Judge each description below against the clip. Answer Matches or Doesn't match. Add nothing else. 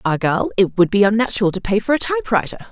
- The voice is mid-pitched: Doesn't match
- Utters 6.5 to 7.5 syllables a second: Matches